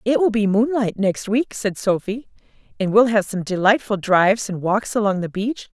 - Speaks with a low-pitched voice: No, high, 210 Hz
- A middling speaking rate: Yes, average, 195 wpm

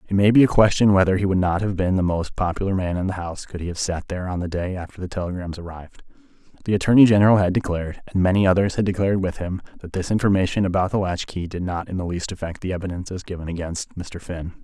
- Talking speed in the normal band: No, fast, 245 wpm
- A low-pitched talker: Yes, very low, 90 Hz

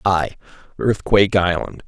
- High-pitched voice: No, very low, 95 Hz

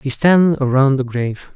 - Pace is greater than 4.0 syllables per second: Yes, 4.9 syllables/s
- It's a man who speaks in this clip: Yes, male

